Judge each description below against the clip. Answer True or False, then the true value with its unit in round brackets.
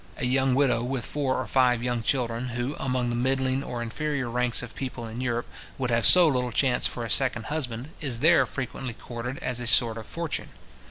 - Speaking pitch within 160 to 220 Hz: False (125 Hz)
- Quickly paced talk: True (210 wpm)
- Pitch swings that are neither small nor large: False (2.0 semitones)